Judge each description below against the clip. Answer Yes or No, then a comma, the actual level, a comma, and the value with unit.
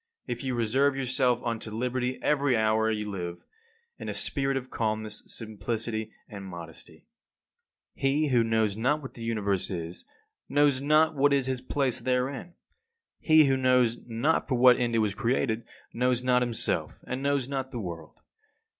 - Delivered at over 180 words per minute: No, average, 165 wpm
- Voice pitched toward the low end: Yes, low, 125 Hz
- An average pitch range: Yes, average, 3.5 semitones